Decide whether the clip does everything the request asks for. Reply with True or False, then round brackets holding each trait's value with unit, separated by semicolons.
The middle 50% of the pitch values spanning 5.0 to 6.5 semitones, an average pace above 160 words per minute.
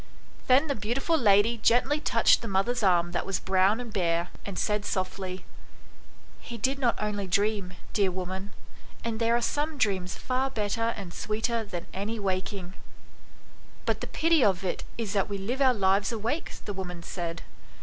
False (3.9 semitones; 175 wpm)